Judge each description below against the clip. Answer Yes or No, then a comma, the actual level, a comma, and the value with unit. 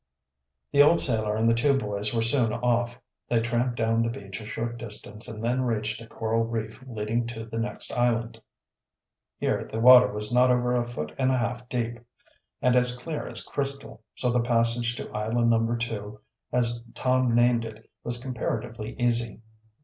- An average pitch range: No, narrow, 1.5 semitones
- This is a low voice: Yes, low, 115 Hz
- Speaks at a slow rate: No, average, 180 wpm